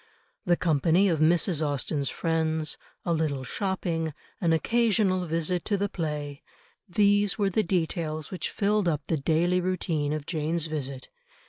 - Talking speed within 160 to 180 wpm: No, average, 145 wpm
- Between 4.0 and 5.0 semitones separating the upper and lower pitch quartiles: No, average, 3.2 semitones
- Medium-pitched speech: Yes, medium, 165 Hz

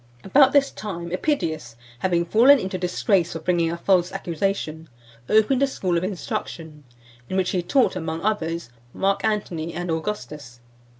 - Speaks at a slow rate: No, average, 160 wpm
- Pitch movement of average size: Yes, average, 4.1 semitones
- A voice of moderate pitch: Yes, medium, 180 Hz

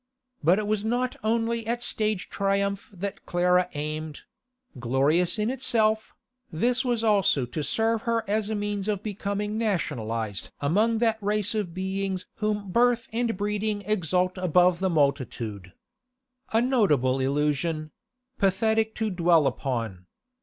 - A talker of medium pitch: No, high, 200 Hz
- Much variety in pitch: Yes, wide, 5.7 semitones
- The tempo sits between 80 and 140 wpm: Yes, slow, 135 wpm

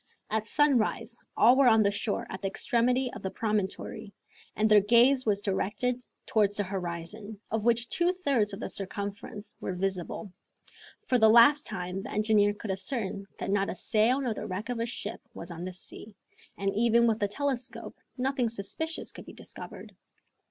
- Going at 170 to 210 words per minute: Yes, average, 180 wpm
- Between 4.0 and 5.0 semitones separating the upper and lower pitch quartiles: No, average, 3.3 semitones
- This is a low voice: No, high, 215 Hz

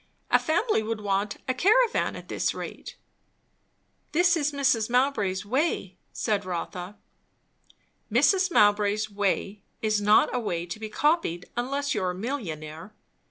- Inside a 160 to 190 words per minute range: No, average, 140 wpm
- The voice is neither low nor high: No, high, 215 Hz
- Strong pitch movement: Yes, wide, 6.2 semitones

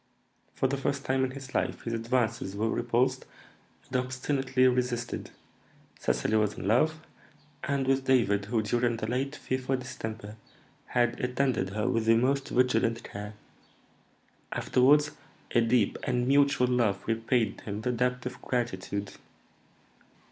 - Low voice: Yes, low, 125 Hz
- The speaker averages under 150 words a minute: Yes, average, 140 wpm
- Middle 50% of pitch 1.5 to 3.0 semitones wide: Yes, average, 2.7 semitones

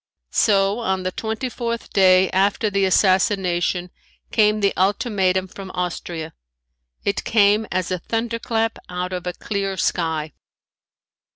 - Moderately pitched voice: No, high, 195 Hz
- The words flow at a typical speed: No, slow, 125 wpm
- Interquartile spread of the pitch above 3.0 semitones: No, average, 2.7 semitones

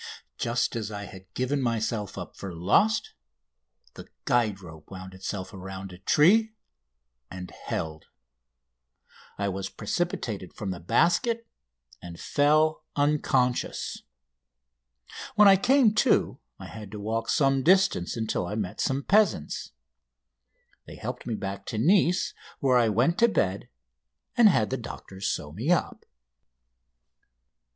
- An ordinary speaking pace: No, slow, 130 wpm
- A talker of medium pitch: No, low, 115 Hz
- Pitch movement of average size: No, wide, 8.4 semitones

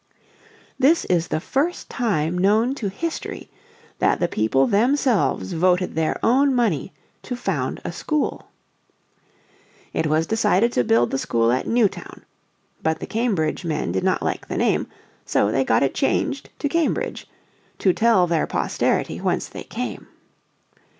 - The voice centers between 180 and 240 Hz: Yes, high, 190 Hz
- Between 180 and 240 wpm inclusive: No, average, 150 wpm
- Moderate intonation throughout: No, wide, 7.8 semitones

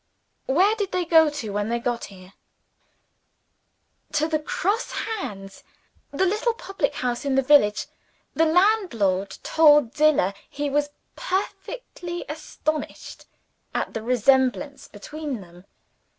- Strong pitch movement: Yes, wide, 7.0 semitones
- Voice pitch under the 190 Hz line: No, very high, 290 Hz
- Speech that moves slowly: Yes, slow, 120 wpm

